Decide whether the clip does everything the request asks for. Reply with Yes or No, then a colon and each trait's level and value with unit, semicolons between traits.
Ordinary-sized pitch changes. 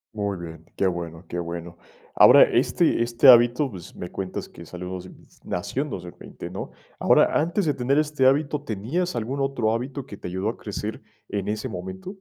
No: wide, 7.2 semitones